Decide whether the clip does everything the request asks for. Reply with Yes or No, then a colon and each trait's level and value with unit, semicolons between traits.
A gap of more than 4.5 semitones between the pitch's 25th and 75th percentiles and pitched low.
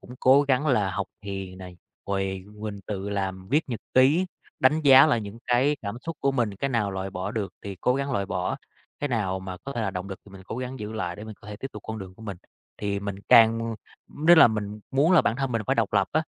Yes: average, 5.1 semitones; low, 110 Hz